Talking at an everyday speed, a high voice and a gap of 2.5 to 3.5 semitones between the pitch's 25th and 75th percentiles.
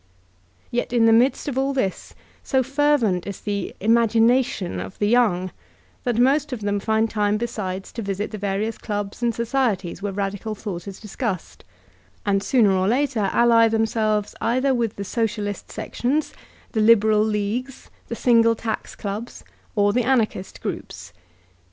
Yes: average, 155 wpm; high, 220 Hz; average, 2.9 semitones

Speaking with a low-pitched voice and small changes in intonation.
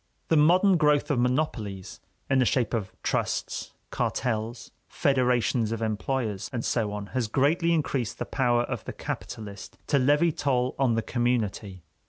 No: low, 125 Hz; average, 4.2 semitones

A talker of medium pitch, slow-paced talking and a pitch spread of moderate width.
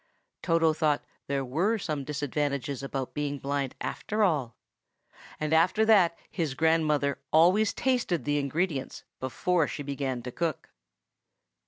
Yes: medium, 150 Hz; slow, 130 wpm; average, 3.4 semitones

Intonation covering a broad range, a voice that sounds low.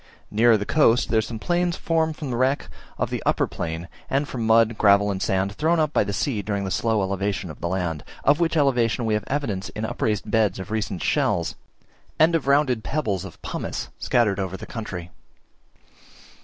Yes: wide, 5.8 semitones; low, 110 Hz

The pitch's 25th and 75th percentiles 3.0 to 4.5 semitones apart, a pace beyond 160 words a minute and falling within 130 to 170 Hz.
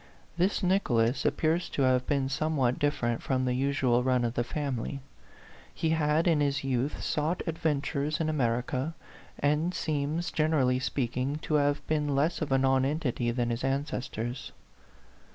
No: average, 3.4 semitones; average, 155 wpm; medium, 140 Hz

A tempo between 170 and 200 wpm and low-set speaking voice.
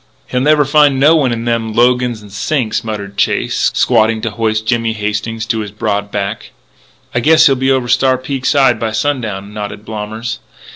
Yes: average, 185 wpm; low, 115 Hz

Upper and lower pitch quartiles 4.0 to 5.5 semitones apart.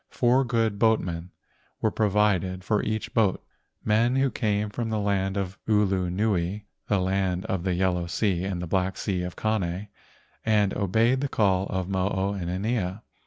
No: average, 2.8 semitones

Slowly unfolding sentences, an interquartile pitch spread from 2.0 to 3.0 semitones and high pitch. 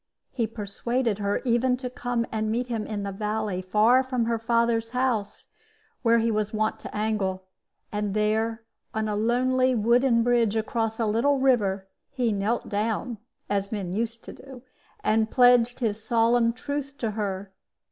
No: average, 165 wpm; narrow, 2.4 semitones; high, 225 Hz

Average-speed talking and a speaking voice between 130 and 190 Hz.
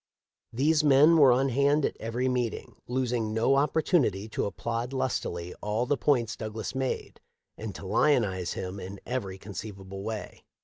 No: average, 150 wpm; low, 115 Hz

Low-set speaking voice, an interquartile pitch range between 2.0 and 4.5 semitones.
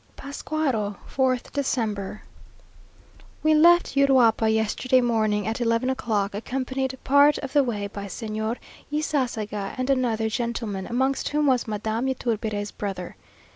No: high, 235 Hz; average, 3.8 semitones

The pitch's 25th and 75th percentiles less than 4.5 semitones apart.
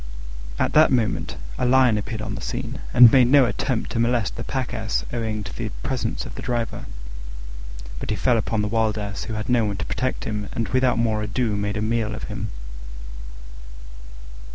Yes: narrow, 2.6 semitones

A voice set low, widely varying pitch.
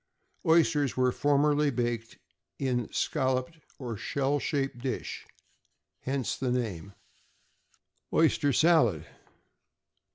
No: low, 130 Hz; average, 3.2 semitones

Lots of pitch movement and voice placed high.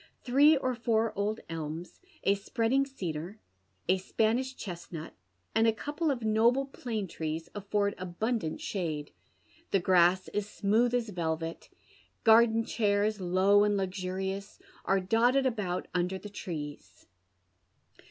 No: average, 4.0 semitones; high, 205 Hz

